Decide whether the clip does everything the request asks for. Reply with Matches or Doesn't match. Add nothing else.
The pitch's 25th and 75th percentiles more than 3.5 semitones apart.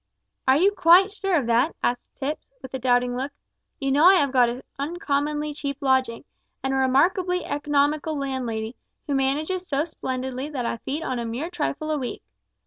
Doesn't match